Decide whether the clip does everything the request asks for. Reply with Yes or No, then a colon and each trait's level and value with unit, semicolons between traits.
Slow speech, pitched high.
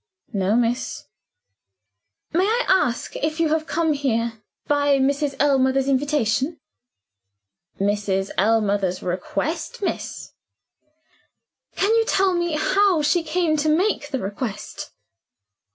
Yes: slow, 115 wpm; very high, 285 Hz